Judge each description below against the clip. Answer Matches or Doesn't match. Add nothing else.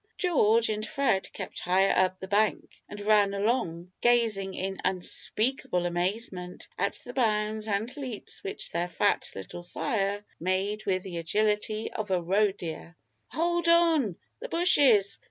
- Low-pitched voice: Doesn't match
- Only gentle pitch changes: Doesn't match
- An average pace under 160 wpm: Matches